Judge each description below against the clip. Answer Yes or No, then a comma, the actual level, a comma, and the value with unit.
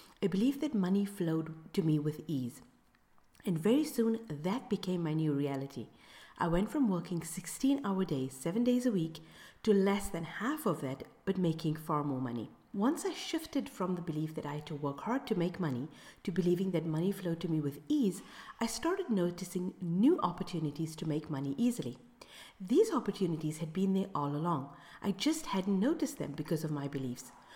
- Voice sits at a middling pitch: Yes, medium, 180 Hz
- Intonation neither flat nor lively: No, wide, 5.8 semitones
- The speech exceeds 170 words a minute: Yes, average, 190 wpm